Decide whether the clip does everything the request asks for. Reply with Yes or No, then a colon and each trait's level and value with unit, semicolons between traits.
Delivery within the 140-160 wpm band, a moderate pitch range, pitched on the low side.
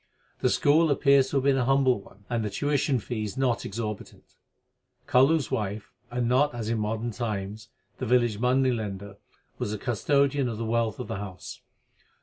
No: average, 180 wpm; average, 3.8 semitones; low, 120 Hz